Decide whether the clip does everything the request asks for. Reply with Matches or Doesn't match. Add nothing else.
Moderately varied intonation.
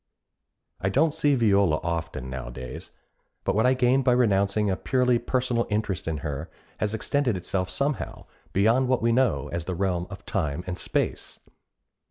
Doesn't match